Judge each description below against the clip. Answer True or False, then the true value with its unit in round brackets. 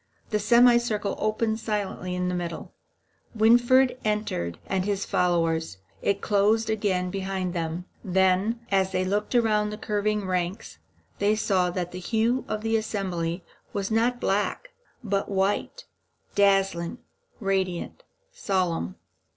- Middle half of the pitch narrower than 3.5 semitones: True (3.1 semitones)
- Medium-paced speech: False (125 wpm)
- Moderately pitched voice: False (200 Hz)